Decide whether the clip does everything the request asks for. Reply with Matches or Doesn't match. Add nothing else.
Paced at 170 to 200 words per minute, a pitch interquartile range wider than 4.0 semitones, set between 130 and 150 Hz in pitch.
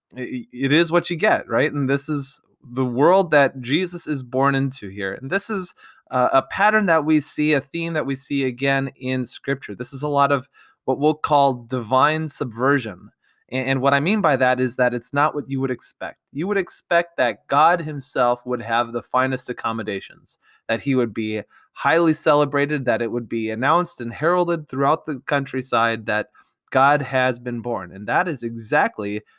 Doesn't match